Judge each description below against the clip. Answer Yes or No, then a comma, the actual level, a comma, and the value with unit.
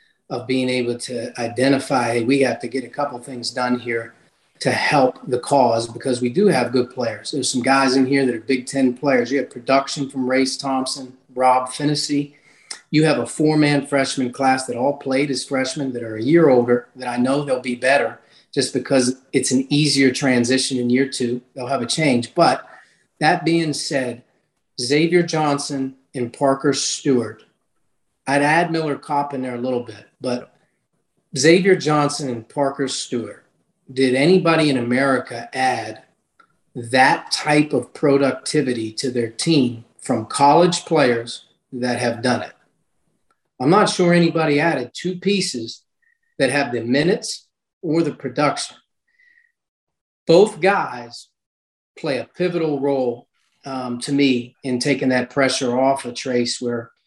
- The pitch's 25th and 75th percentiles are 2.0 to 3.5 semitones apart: Yes, average, 2.7 semitones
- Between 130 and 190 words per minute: Yes, average, 160 wpm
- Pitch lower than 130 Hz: No, low, 135 Hz